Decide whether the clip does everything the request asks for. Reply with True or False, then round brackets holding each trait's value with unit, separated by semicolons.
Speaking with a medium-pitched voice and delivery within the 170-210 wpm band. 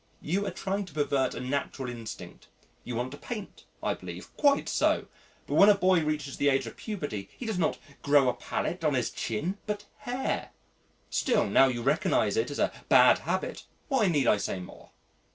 True (150 Hz; 195 wpm)